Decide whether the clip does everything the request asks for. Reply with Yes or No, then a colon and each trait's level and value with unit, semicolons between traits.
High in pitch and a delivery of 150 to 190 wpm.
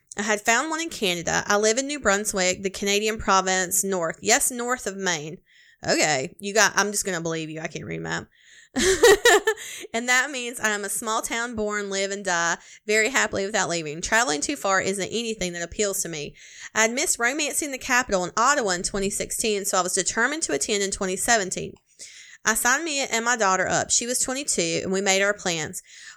No: high, 205 Hz; fast, 205 wpm